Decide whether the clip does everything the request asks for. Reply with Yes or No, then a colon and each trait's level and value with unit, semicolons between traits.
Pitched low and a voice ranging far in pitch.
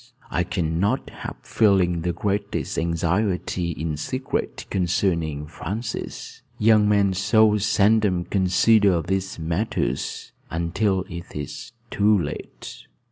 No: very low, 95 Hz; average, 3.7 semitones